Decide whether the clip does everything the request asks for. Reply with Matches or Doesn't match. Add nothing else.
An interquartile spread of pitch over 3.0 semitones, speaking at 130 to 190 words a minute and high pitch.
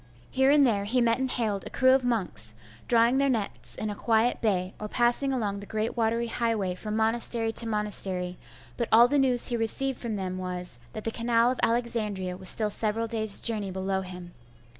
Doesn't match